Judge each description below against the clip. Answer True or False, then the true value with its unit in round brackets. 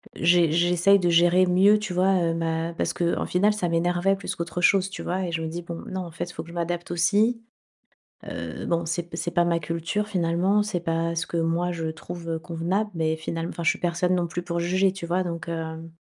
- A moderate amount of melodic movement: False (1.6 semitones)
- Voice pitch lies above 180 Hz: False (175 Hz)